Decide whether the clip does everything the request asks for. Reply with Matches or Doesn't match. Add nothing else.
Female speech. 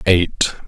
Doesn't match